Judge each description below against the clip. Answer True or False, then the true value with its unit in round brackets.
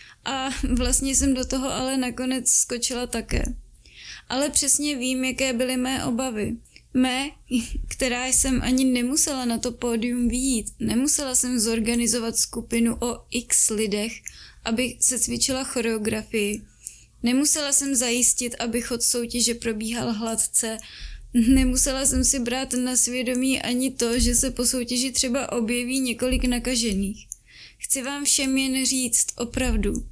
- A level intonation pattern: True (1.8 semitones)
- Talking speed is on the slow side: False (130 wpm)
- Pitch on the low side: False (250 Hz)